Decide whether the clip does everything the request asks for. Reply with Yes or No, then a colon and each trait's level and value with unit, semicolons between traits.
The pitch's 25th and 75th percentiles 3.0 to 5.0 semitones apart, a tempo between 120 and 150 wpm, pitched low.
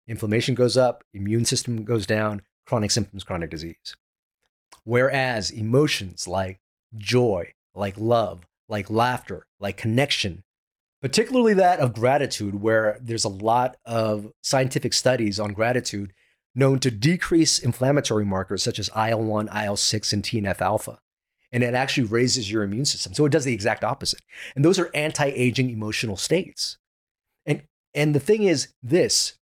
Yes: average, 3.7 semitones; average, 145 wpm; low, 115 Hz